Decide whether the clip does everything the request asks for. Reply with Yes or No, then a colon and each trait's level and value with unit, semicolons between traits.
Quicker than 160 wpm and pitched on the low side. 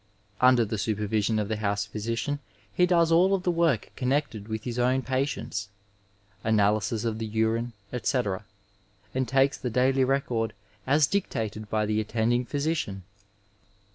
No: average, 145 wpm; low, 115 Hz